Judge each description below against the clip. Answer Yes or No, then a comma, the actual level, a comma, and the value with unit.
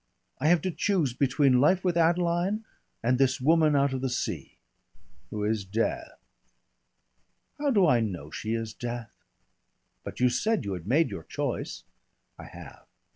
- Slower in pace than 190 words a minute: Yes, average, 160 wpm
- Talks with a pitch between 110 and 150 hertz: Yes, low, 135 Hz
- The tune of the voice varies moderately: No, wide, 7.1 semitones